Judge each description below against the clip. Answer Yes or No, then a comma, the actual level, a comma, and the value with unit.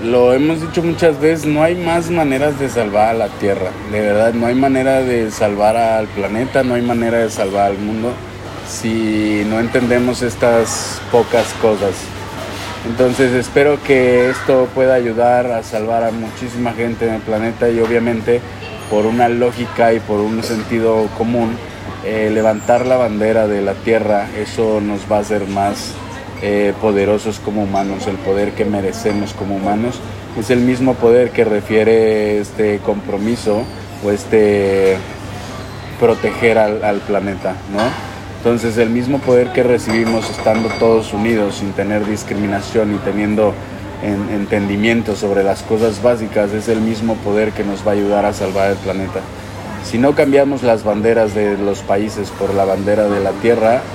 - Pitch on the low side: Yes, low, 110 Hz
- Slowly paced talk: No, average, 160 wpm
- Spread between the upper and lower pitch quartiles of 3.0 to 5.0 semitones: No, narrow, 2.6 semitones